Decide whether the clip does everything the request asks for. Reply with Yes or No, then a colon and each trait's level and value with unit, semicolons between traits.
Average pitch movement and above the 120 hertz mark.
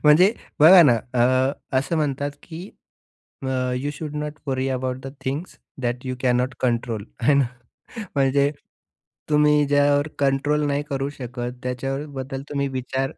No: narrow, 2.3 semitones; low, 135 Hz